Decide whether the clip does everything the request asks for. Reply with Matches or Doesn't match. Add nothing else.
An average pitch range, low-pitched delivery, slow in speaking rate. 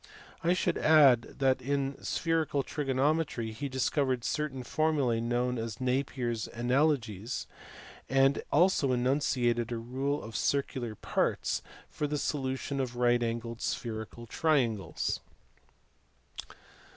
Matches